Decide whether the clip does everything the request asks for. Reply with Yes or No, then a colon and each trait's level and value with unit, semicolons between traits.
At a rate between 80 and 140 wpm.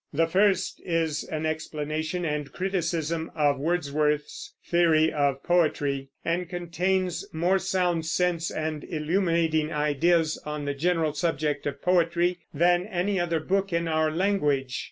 Yes: slow, 135 wpm